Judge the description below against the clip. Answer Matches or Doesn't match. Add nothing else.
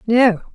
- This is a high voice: Matches